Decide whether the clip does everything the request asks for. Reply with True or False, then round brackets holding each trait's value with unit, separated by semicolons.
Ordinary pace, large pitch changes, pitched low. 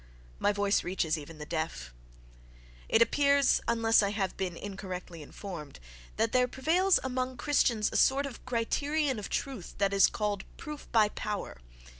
False (150 wpm; 7.2 semitones; 205 Hz)